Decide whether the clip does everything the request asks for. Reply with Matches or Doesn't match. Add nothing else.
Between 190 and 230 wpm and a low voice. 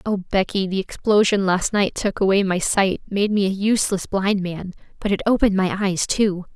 Doesn't match